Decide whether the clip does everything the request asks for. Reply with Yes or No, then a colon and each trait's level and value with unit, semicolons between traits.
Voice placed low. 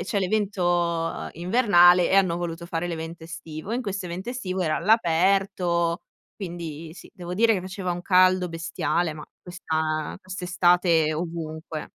No: medium, 175 Hz